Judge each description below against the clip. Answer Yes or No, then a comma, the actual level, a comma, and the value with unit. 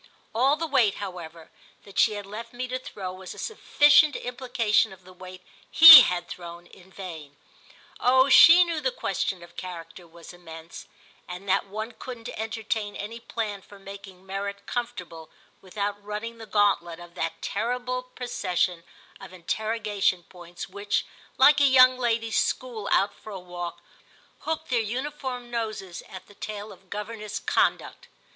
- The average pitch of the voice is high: Yes, high, 205 Hz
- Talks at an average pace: Yes, average, 155 wpm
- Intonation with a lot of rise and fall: No, average, 4.8 semitones